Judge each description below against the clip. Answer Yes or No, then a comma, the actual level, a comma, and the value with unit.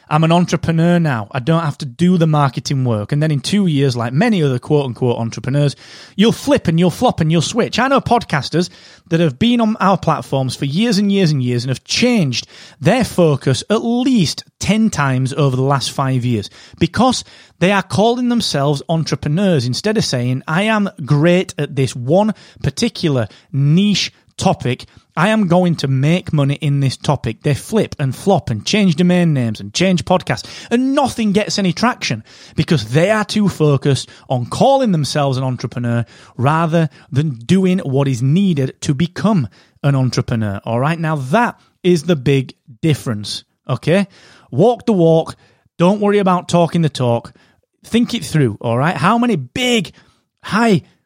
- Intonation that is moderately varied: No, wide, 6.0 semitones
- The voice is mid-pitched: Yes, medium, 155 Hz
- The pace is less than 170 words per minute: No, average, 175 wpm